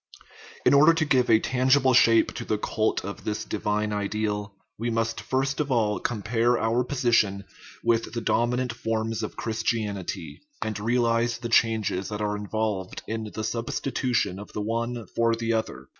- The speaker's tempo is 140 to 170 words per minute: Yes, average, 165 wpm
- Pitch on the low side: Yes, low, 115 Hz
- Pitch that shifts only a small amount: Yes, narrow, 2.2 semitones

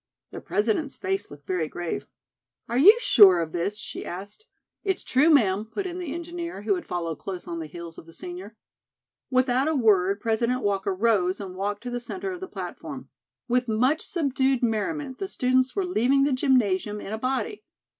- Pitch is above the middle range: Yes, high, 235 Hz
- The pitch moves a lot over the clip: Yes, wide, 6.4 semitones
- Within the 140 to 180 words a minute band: No, average, 190 wpm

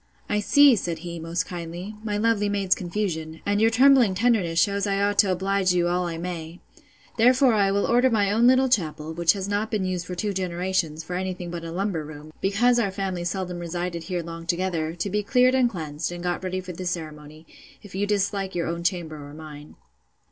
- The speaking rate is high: Yes, fast, 215 wpm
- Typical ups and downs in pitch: Yes, average, 3.3 semitones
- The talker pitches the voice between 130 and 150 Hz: No, medium, 185 Hz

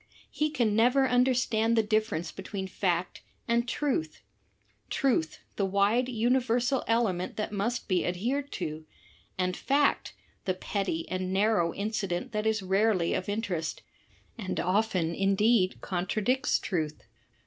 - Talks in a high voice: Yes, high, 210 Hz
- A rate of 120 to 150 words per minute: Yes, slow, 135 wpm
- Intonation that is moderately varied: Yes, average, 4.4 semitones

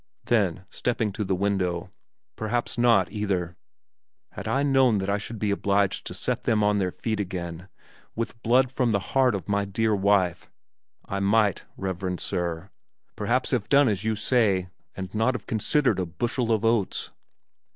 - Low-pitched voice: Yes, low, 105 Hz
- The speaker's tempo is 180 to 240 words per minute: No, average, 170 wpm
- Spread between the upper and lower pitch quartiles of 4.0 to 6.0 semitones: No, average, 3.4 semitones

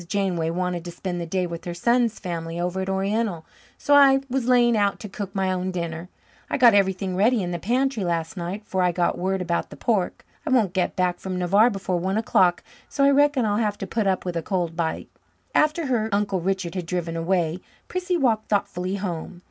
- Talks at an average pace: No, fast, 220 wpm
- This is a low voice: No, high, 190 Hz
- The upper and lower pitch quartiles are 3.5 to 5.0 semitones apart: Yes, average, 3.8 semitones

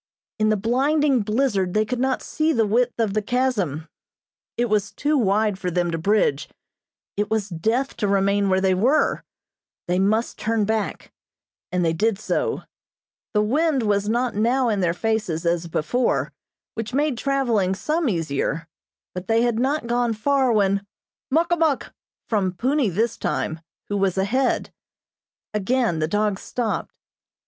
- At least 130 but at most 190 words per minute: Yes, average, 160 wpm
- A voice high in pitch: Yes, high, 215 Hz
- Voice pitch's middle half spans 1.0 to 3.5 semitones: No, average, 4.5 semitones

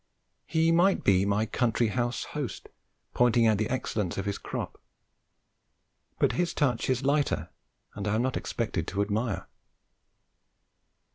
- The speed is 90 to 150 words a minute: Yes, average, 140 wpm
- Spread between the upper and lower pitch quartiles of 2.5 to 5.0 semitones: Yes, average, 4.1 semitones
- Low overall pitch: Yes, low, 115 Hz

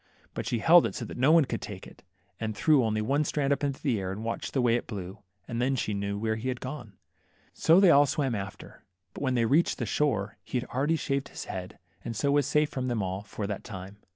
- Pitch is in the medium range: No, low, 125 Hz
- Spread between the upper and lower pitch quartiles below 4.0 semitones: No, wide, 5.4 semitones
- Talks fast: Yes, fast, 255 wpm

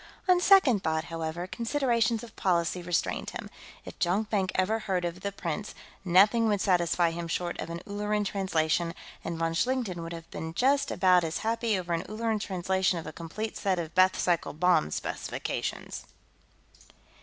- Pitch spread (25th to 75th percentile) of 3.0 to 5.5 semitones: Yes, average, 4.1 semitones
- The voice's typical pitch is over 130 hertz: Yes, medium, 185 Hz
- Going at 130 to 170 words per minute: Yes, average, 165 wpm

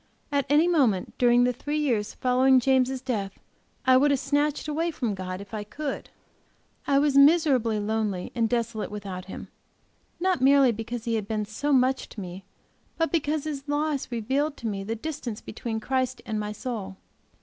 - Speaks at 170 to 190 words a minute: Yes, average, 180 wpm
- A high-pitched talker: Yes, very high, 250 Hz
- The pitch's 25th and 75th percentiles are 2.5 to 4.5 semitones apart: No, average, 4.9 semitones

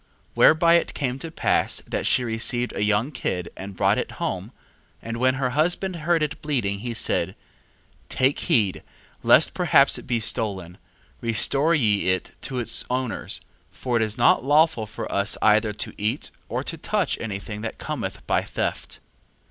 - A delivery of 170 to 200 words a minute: Yes, average, 180 wpm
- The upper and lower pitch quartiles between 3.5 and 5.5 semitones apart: Yes, average, 5.2 semitones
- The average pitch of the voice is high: No, low, 120 Hz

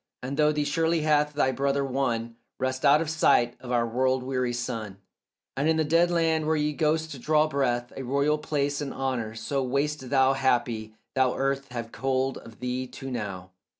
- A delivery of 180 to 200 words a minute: Yes, average, 190 wpm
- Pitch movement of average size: Yes, average, 3.3 semitones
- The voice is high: No, low, 135 Hz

